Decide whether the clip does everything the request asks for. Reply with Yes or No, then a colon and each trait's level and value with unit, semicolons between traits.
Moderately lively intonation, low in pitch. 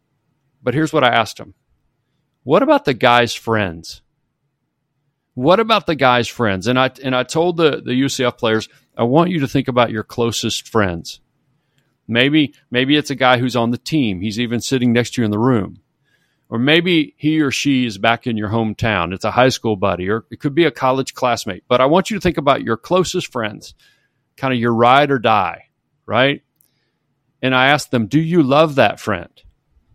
Yes: average, 3.7 semitones; low, 130 Hz